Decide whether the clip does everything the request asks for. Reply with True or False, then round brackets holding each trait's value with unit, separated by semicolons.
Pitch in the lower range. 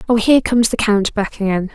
False (220 Hz)